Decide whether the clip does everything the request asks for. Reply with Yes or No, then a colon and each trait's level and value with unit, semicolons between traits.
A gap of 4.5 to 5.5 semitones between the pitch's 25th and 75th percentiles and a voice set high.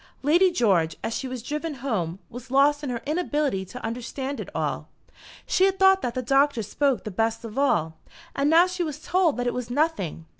Yes: average, 4.8 semitones; very high, 270 Hz